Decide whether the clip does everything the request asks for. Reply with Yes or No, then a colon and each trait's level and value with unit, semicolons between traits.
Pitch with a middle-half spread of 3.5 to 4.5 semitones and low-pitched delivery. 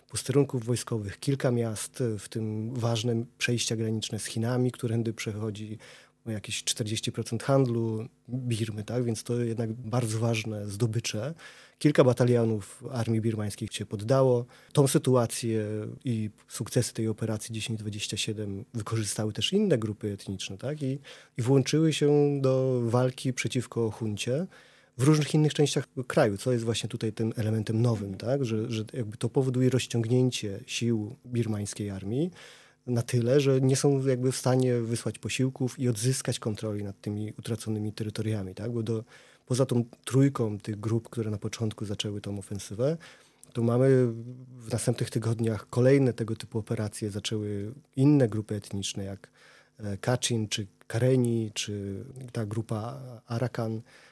No: narrow, 2.6 semitones; low, 115 Hz